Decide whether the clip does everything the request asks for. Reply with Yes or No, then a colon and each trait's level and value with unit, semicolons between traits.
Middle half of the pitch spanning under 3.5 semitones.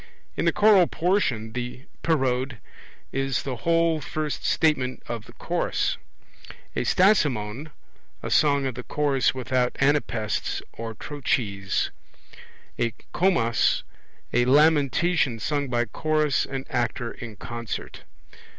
No: average, 4.4 semitones